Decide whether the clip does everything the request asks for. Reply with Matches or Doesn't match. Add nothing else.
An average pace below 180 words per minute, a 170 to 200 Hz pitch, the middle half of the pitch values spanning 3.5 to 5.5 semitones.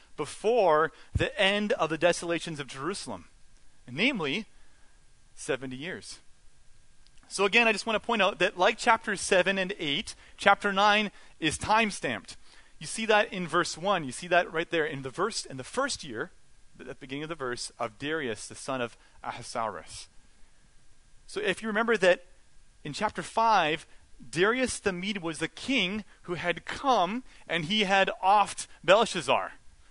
Matches